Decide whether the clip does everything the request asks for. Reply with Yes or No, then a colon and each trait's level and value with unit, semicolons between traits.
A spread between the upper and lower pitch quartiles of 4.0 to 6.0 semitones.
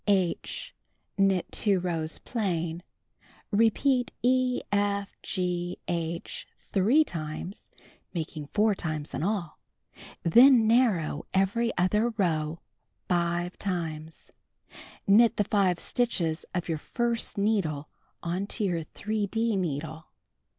Yes: average, 4.5 semitones